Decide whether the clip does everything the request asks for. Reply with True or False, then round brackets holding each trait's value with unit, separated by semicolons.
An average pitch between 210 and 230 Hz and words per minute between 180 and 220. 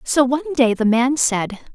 False (255 Hz; 205 wpm)